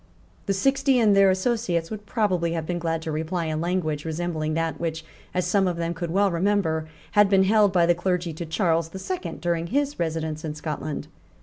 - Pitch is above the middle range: No, medium, 175 Hz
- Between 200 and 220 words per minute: Yes, fast, 205 wpm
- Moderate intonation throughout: Yes, average, 3.4 semitones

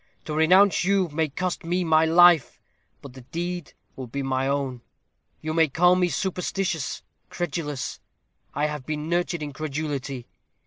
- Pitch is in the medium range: Yes, medium, 155 Hz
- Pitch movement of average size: Yes, average, 3.9 semitones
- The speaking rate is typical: Yes, average, 150 wpm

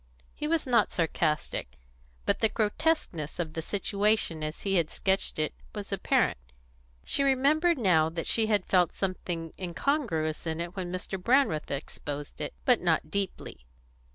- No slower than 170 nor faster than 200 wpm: No, average, 155 wpm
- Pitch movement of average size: No, wide, 5.8 semitones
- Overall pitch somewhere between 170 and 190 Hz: Yes, medium, 185 Hz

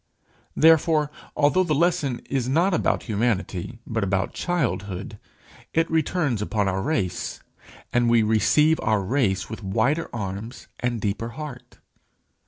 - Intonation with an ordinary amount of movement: No, wide, 6.7 semitones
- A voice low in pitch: Yes, low, 120 Hz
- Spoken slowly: Yes, slow, 130 wpm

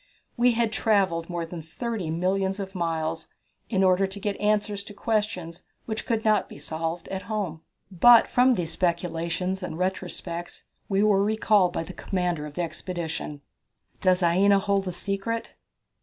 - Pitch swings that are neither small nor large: Yes, average, 3.5 semitones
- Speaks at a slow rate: No, average, 160 wpm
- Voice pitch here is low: No, high, 190 Hz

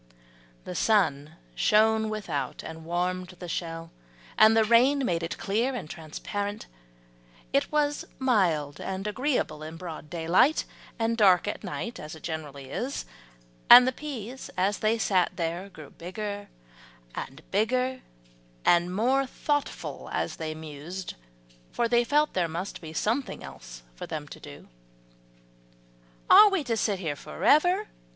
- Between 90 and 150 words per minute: Yes, average, 145 wpm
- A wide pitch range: Yes, wide, 6.6 semitones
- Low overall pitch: No, high, 190 Hz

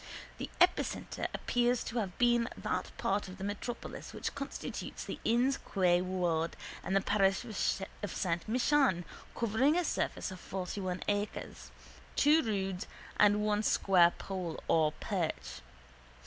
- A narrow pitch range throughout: No, average, 4.5 semitones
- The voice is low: No, high, 205 Hz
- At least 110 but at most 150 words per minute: Yes, slow, 135 wpm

